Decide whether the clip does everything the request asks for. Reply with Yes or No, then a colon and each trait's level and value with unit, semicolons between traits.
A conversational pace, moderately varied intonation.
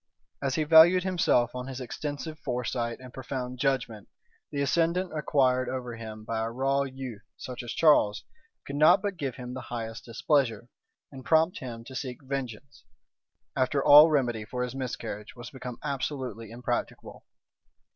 Yes: average, 155 wpm; average, 3.1 semitones